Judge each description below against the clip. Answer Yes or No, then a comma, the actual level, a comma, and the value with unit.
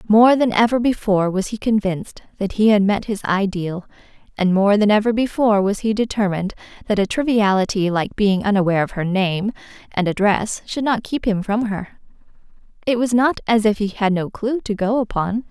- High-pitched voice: Yes, high, 210 Hz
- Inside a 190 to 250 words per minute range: Yes, average, 195 wpm